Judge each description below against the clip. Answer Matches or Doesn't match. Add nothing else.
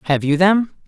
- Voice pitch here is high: Doesn't match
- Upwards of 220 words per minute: Doesn't match